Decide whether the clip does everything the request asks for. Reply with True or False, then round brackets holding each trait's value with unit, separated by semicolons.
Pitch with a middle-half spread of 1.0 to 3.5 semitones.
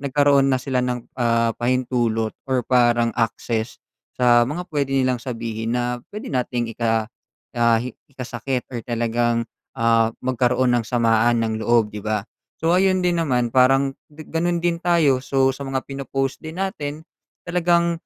True (3.1 semitones)